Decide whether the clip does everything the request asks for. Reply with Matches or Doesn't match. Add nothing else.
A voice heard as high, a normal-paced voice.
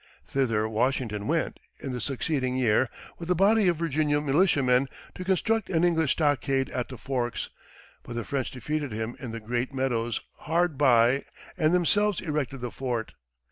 Doesn't match